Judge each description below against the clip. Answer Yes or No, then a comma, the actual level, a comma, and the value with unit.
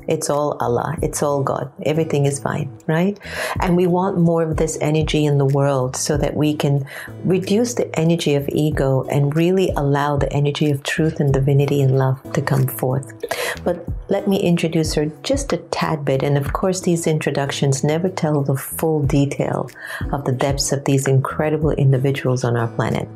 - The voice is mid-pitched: Yes, medium, 145 Hz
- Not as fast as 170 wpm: No, average, 185 wpm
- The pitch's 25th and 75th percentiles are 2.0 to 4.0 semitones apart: Yes, narrow, 2.6 semitones